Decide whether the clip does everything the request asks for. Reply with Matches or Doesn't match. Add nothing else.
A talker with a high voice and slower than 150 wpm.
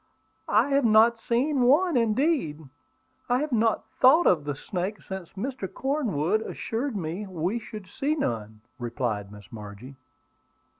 Matches